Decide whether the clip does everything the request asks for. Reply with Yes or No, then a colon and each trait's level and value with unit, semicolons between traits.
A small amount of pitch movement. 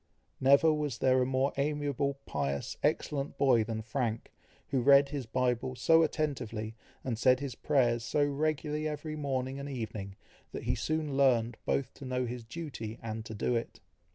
No: average, 3.6 semitones